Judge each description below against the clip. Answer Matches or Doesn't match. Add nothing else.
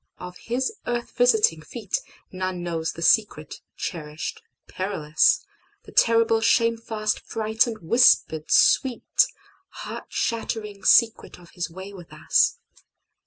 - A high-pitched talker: Matches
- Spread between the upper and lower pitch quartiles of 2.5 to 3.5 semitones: Doesn't match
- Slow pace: Matches